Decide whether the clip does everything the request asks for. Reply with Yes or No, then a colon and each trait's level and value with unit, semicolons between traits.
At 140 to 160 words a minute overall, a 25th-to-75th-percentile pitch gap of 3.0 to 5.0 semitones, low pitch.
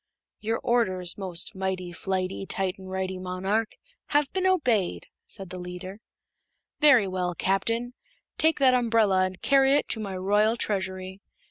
No: average, 145 wpm; average, 3.6 semitones; high, 195 Hz